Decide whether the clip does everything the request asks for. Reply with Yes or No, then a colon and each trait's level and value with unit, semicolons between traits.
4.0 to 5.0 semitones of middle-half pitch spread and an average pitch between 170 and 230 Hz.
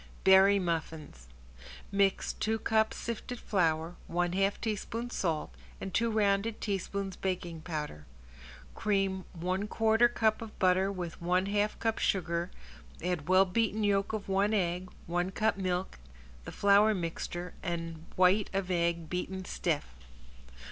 No: average, 3.0 semitones; high, 190 Hz